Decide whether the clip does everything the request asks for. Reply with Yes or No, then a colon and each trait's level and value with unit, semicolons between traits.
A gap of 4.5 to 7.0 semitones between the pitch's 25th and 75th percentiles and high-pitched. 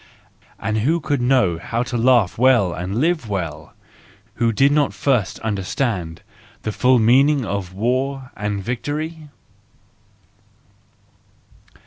No: average, 5.2 semitones; low, 120 Hz